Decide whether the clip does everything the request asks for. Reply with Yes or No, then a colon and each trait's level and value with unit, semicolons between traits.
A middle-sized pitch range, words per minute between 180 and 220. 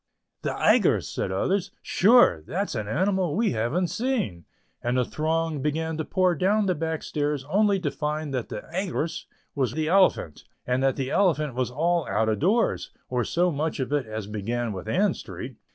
No: wide, 6.6 semitones; average, 185 wpm